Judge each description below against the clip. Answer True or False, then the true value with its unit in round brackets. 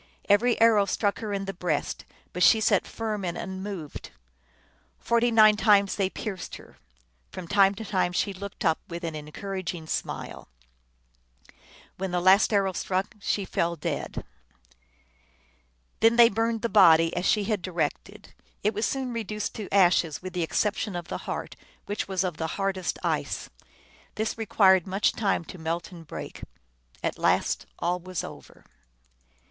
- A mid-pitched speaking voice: False (195 Hz)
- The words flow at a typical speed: True (160 wpm)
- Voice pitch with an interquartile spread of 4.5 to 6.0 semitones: False (3.1 semitones)